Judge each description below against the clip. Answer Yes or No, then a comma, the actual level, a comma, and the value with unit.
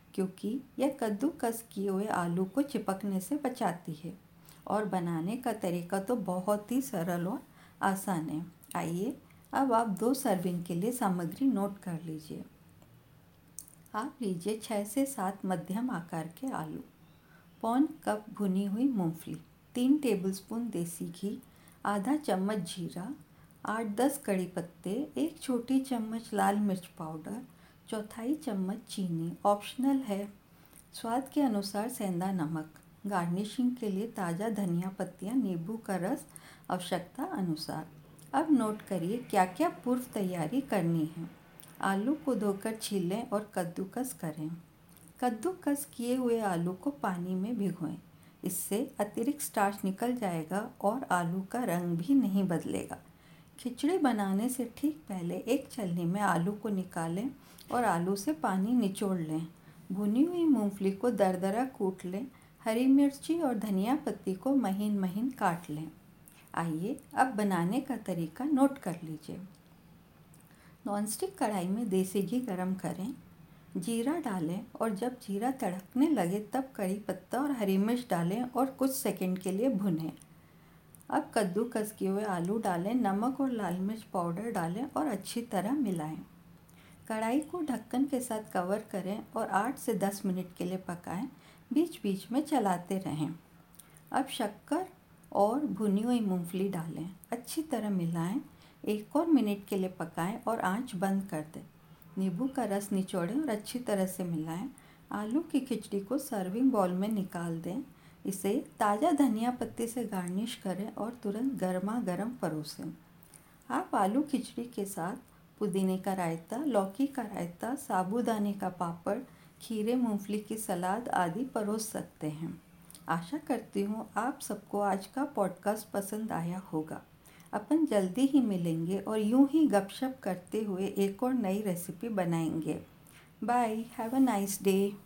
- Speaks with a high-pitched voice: Yes, high, 205 Hz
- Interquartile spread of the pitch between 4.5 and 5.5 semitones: Yes, average, 5.0 semitones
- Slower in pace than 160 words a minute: Yes, average, 145 wpm